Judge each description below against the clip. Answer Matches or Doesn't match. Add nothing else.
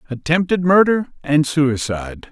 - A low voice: Doesn't match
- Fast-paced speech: Doesn't match